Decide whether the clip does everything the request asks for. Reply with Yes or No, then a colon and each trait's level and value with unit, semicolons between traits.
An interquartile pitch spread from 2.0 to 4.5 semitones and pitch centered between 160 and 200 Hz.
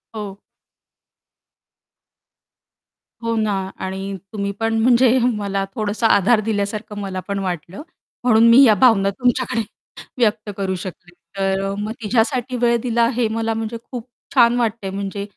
No: average, 2.8 semitones; high, 215 Hz